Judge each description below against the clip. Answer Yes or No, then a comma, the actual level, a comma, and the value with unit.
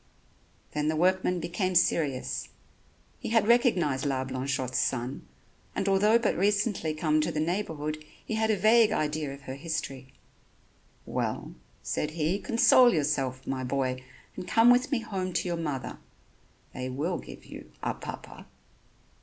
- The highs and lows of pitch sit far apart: Yes, wide, 6.6 semitones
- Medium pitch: Yes, medium, 160 Hz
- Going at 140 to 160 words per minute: Yes, average, 150 wpm